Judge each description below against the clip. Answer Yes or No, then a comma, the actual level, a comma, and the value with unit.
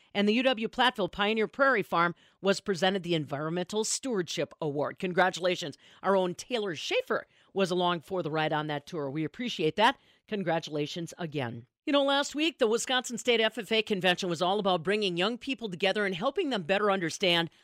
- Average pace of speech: Yes, average, 175 wpm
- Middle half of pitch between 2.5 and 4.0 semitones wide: No, average, 4.4 semitones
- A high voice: Yes, high, 195 Hz